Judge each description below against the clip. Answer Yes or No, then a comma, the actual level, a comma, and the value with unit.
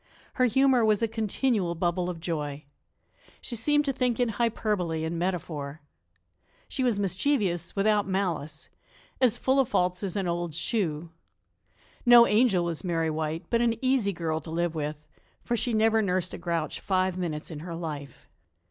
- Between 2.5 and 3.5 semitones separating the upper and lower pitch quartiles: No, wide, 5.5 semitones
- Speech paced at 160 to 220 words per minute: Yes, average, 165 wpm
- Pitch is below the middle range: No, medium, 185 Hz